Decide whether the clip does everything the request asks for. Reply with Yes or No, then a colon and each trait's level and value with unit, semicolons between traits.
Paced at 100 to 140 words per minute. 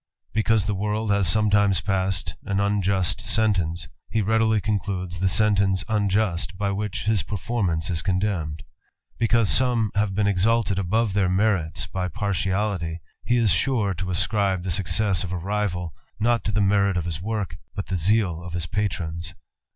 Yes: slow, 135 wpm